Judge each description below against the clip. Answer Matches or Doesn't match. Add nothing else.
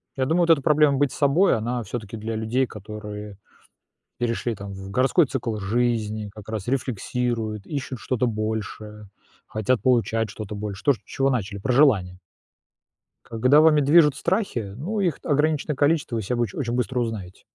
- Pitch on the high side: Doesn't match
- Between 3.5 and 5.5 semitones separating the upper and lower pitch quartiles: Matches